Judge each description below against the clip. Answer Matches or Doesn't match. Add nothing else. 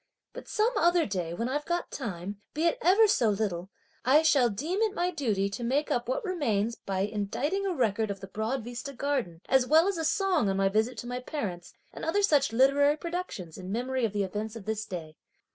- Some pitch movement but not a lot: Doesn't match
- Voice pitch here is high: Matches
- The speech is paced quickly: Matches